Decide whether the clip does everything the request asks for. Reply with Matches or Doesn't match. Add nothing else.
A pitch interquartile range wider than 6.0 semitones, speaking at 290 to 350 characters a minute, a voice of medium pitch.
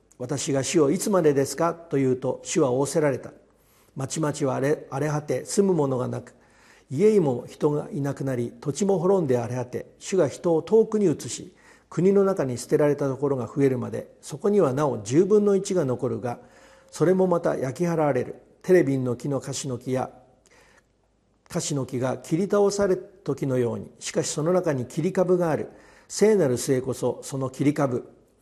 Doesn't match